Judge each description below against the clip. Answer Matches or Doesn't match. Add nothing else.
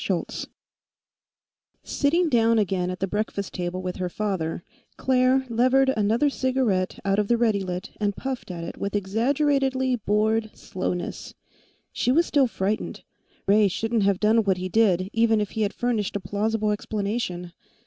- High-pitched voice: Matches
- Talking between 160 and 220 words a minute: Doesn't match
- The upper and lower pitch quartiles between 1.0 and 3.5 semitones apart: Doesn't match